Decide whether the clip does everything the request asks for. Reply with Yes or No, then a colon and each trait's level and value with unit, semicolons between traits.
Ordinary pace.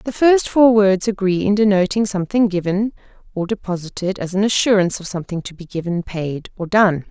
Yes: average, 185 wpm